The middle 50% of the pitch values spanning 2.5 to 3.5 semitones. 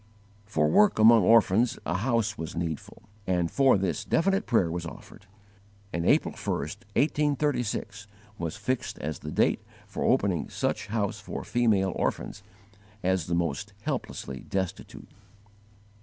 No: average, 5.3 semitones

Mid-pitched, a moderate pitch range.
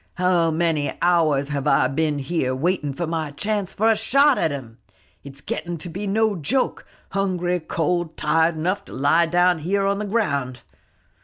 Yes: medium, 170 Hz; average, 4.3 semitones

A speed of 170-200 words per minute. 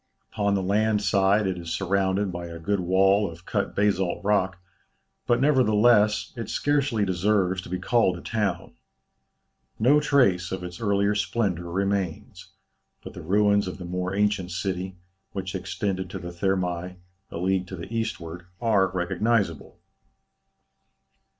No: average, 145 wpm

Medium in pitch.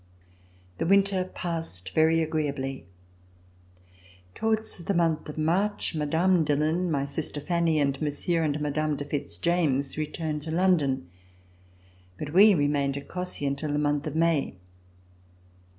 Yes: medium, 155 Hz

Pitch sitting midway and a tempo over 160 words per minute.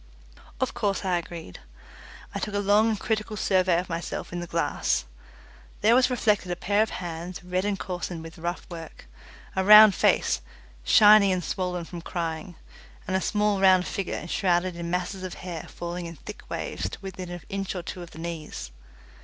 Yes: medium, 180 Hz; average, 185 wpm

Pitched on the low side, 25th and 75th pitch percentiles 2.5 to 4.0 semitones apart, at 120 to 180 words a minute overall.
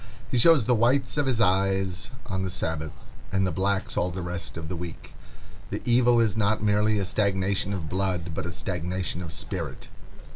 No: very low, 95 Hz; average, 3.3 semitones; average, 190 wpm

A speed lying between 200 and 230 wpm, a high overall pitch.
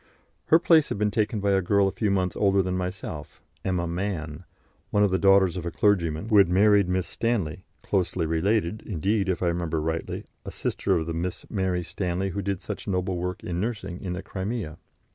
No: fast, 205 wpm; very low, 95 Hz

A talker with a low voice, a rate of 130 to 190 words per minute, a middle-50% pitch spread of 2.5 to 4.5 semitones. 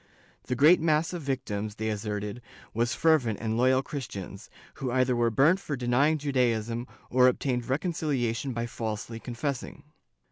Yes: low, 125 Hz; average, 145 wpm; average, 3.7 semitones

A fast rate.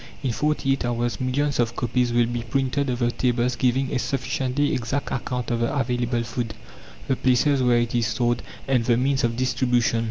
No: average, 195 wpm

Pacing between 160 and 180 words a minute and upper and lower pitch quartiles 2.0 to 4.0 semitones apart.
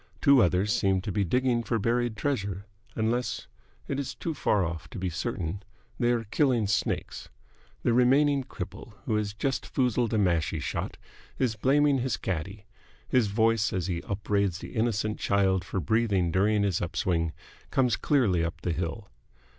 No: average, 170 wpm; average, 4.4 semitones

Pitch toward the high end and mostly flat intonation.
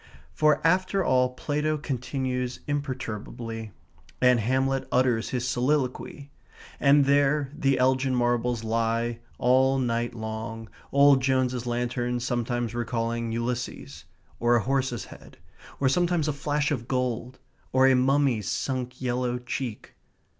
No: low, 125 Hz; narrow, 2.3 semitones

